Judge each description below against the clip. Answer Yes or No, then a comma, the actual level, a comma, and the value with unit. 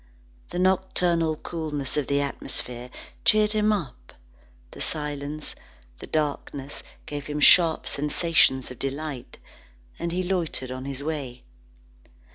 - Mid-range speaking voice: Yes, medium, 150 Hz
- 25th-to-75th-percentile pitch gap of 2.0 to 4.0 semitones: Yes, average, 3.6 semitones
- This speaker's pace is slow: Yes, slow, 120 wpm